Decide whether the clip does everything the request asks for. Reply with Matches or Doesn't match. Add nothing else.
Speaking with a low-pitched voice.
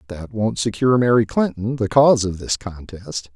Matches